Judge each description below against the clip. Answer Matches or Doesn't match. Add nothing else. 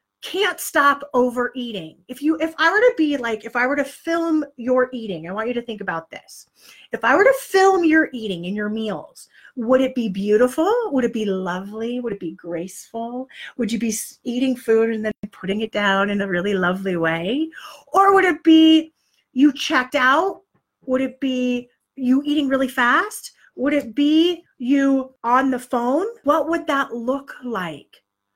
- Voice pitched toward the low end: Doesn't match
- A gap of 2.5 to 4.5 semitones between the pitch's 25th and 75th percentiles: Doesn't match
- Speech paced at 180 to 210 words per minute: Matches